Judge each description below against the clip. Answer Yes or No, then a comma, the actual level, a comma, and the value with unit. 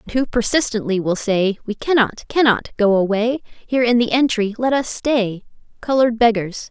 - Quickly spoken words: No, average, 170 wpm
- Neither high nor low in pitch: No, high, 230 Hz